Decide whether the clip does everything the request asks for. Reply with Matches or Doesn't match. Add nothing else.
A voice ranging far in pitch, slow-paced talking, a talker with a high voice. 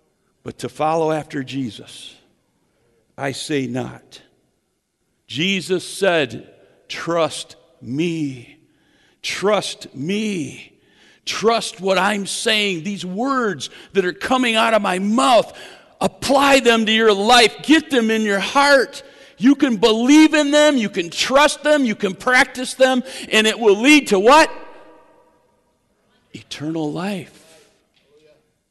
Matches